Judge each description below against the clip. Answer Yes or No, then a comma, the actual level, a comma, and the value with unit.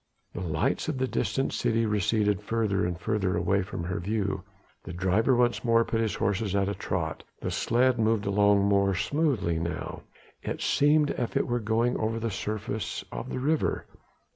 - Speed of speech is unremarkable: Yes, average, 185 wpm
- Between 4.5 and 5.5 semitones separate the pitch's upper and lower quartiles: No, average, 3.3 semitones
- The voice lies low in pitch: Yes, low, 105 Hz